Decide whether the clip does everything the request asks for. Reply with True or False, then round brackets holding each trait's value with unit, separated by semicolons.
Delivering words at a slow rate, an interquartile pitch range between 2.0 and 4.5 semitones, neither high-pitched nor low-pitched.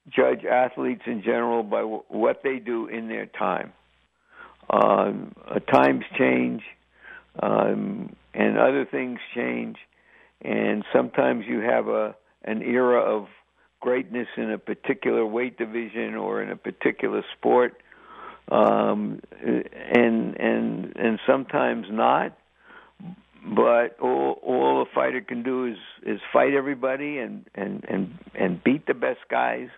False (130 wpm; 2.8 semitones; 120 Hz)